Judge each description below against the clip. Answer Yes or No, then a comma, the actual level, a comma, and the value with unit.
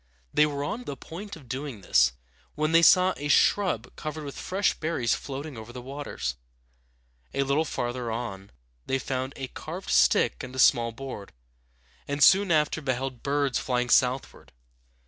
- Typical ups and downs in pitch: Yes, average, 4.0 semitones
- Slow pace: No, average, 165 wpm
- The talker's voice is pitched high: No, low, 135 Hz